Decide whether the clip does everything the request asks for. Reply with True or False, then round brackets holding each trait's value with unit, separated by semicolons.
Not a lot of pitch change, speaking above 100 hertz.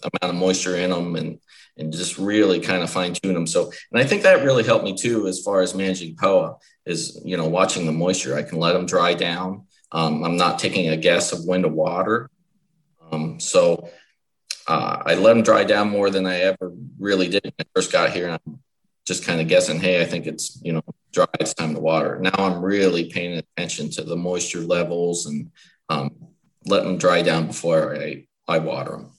False (2.0 semitones; 90 Hz)